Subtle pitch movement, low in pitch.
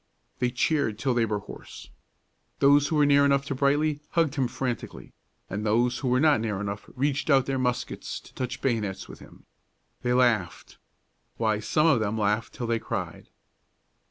No: average, 4.1 semitones; low, 125 Hz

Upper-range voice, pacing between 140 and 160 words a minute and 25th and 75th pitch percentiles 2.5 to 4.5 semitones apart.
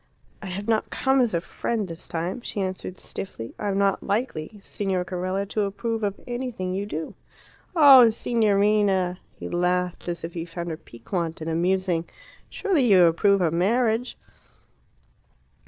Yes: high, 195 Hz; average, 155 wpm; average, 3.8 semitones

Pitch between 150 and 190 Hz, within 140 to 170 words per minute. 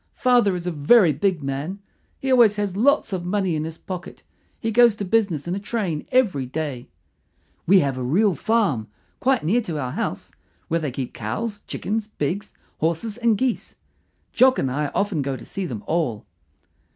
No: medium, 185 Hz; average, 185 wpm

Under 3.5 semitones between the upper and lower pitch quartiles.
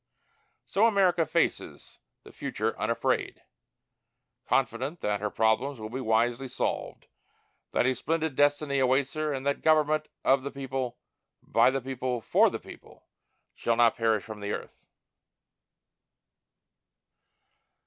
No: average, 3.8 semitones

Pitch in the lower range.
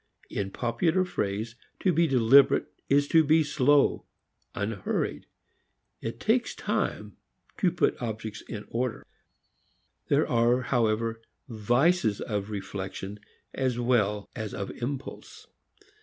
Yes: low, 120 Hz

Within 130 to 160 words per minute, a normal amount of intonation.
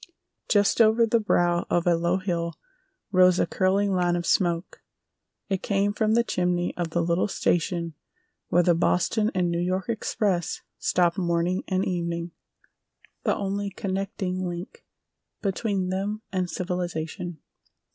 No: average, 140 wpm; narrow, 2.3 semitones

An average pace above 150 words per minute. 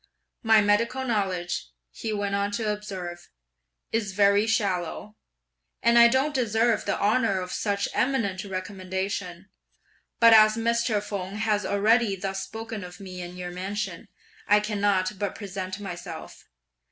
No: average, 140 wpm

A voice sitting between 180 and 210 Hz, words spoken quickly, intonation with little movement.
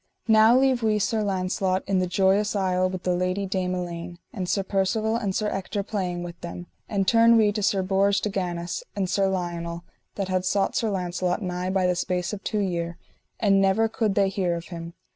Yes: high, 190 Hz; fast, 210 wpm; narrow, 2.2 semitones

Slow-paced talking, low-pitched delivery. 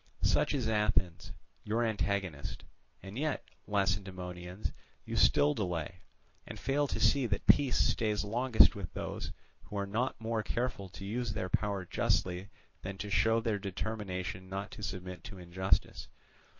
No: average, 150 wpm; low, 100 Hz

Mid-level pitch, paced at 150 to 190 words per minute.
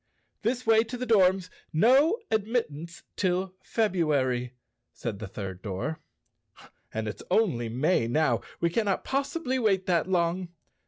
No: medium, 180 Hz; average, 140 wpm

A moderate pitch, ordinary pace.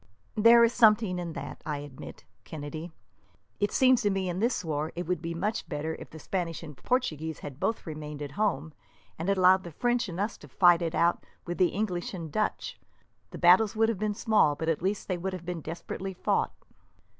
No: medium, 180 Hz; fast, 210 wpm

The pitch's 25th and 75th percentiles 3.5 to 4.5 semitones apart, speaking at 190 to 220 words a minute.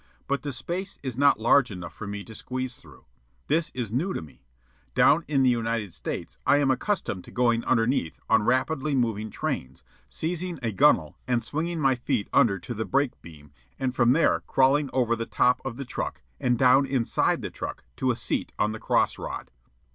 Yes: average, 3.8 semitones; average, 200 wpm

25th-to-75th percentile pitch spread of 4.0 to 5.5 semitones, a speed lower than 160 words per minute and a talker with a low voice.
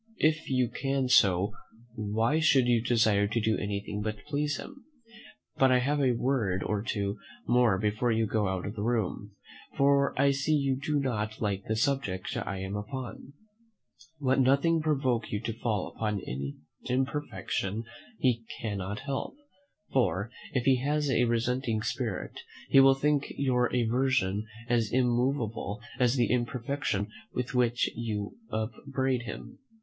Yes: average, 4.3 semitones; average, 150 wpm; low, 120 Hz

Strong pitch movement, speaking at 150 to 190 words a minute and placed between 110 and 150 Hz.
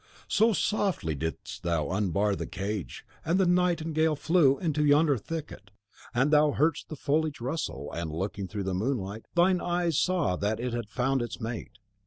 Yes: wide, 8.2 semitones; average, 170 wpm; low, 135 Hz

